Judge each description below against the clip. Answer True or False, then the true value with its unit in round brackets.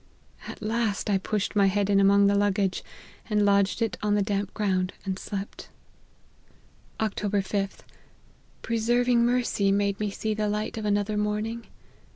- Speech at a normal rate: True (160 wpm)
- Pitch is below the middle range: False (205 Hz)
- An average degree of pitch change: False (1.4 semitones)